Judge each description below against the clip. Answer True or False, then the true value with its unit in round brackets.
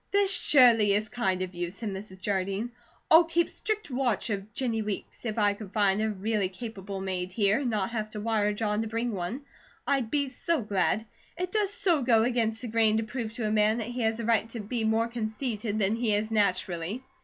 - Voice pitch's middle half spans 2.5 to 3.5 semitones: True (2.8 semitones)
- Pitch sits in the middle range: False (220 Hz)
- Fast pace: True (220 wpm)